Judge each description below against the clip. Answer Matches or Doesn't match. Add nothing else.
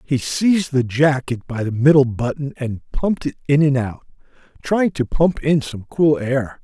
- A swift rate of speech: Doesn't match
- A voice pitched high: Doesn't match